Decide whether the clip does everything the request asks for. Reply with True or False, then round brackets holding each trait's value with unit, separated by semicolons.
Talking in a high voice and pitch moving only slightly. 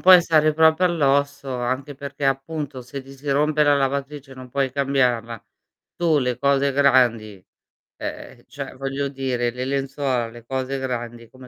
False (135 Hz; 2.0 semitones)